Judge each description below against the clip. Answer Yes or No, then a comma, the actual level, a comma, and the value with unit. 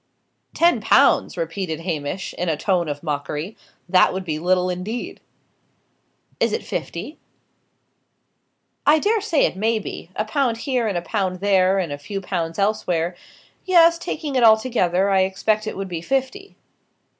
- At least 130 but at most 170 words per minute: Yes, average, 155 wpm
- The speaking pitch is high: Yes, high, 195 Hz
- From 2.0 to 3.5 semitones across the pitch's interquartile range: No, average, 5.1 semitones